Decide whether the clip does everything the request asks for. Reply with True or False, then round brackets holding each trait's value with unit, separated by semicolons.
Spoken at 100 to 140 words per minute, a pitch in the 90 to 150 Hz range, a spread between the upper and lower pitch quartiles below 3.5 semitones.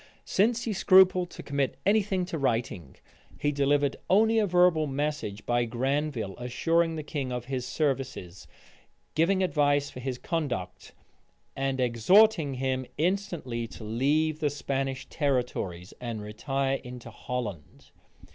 False (135 wpm; 140 Hz; 4.9 semitones)